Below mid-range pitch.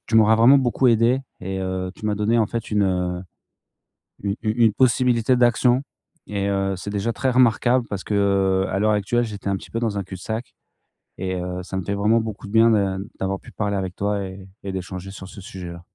Yes: low, 100 Hz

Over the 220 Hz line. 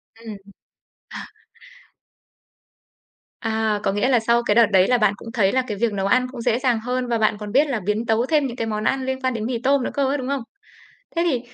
Yes: high, 235 Hz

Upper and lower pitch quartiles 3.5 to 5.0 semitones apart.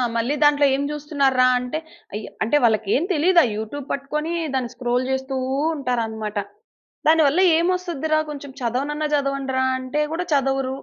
No: average, 2.9 semitones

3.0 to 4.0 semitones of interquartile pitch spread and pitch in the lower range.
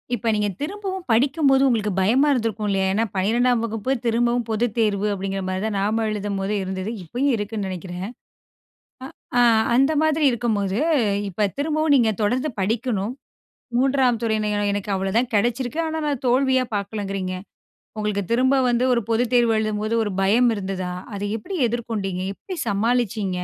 No: average, 3.7 semitones; high, 225 Hz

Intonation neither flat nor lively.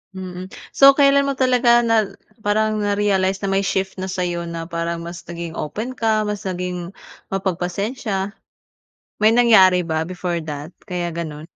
Yes: average, 3.9 semitones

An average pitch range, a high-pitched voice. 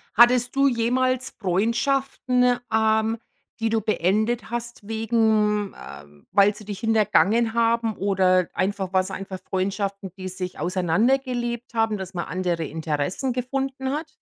Yes: average, 3.9 semitones; high, 220 Hz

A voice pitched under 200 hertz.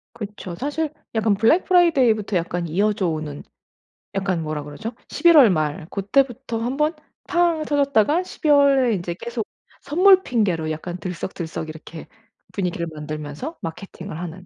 No: high, 205 Hz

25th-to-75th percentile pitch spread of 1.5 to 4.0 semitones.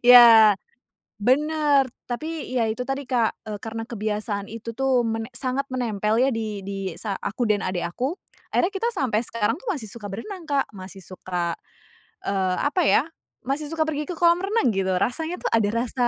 No: average, 5.3 semitones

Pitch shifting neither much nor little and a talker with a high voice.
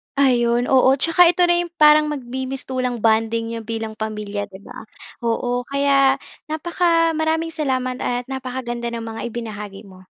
Yes: average, 3.9 semitones; very high, 250 Hz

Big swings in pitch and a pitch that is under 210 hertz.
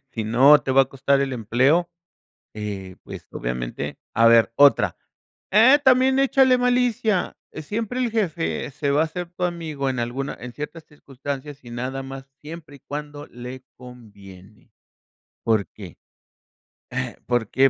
Yes: wide, 6.1 semitones; low, 135 Hz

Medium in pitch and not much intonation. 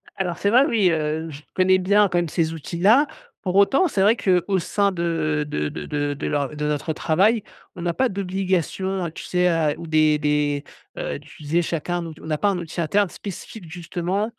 No: medium, 175 Hz; average, 3.9 semitones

